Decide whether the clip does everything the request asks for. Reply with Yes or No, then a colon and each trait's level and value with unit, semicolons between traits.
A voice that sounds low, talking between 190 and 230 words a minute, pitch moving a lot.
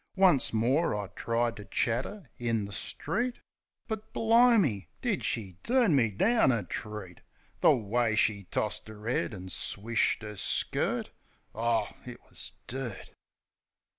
No: low, 115 Hz; average, 140 wpm; wide, 5.9 semitones